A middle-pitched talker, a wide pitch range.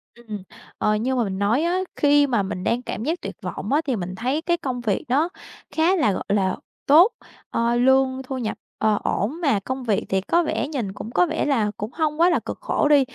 No: very high, 255 Hz; wide, 6.1 semitones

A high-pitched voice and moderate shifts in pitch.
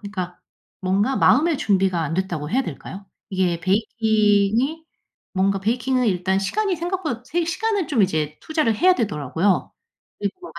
No: high, 205 Hz; wide, 7.2 semitones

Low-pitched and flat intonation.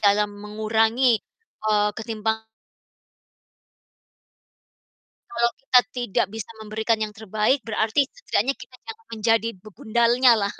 No: high, 220 Hz; narrow, 2.2 semitones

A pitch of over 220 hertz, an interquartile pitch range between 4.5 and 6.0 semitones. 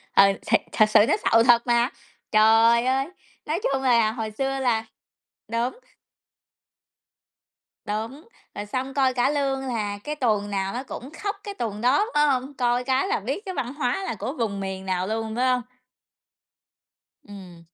No: high, 240 Hz; average, 3.8 semitones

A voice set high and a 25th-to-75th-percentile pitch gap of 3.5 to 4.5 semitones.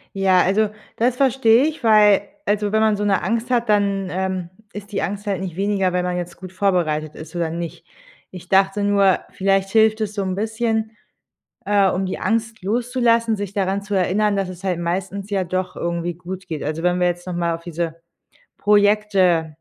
No: high, 195 Hz; average, 2.8 semitones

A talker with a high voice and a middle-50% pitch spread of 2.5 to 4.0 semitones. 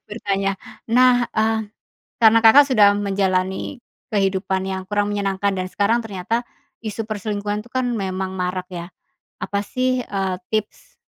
Yes: high, 205 Hz; average, 2.8 semitones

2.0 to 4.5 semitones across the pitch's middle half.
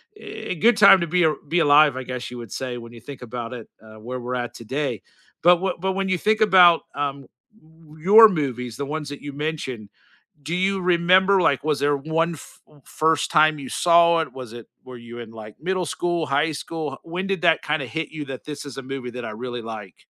No: wide, 5.4 semitones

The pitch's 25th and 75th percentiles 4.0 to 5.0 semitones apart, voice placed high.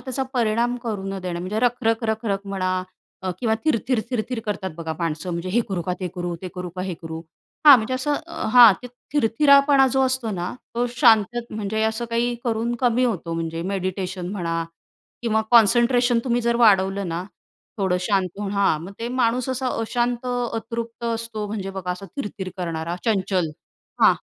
Yes: average, 4.4 semitones; high, 220 Hz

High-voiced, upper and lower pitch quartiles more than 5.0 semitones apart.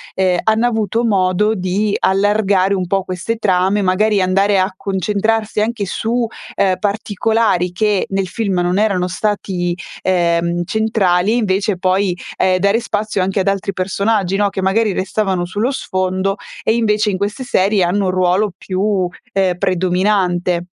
No: high, 195 Hz; narrow, 2.4 semitones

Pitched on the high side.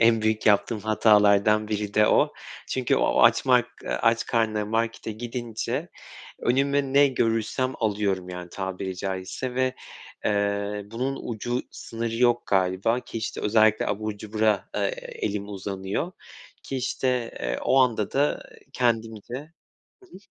No: low, 110 Hz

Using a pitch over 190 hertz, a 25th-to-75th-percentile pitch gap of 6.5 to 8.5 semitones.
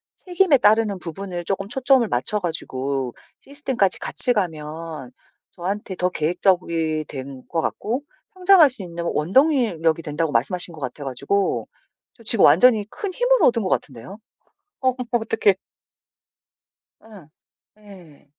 No: medium, 185 Hz; wide, 6.9 semitones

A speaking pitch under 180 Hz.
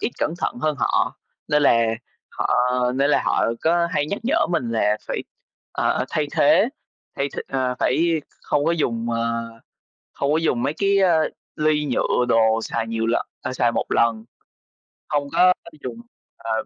Yes: medium, 140 Hz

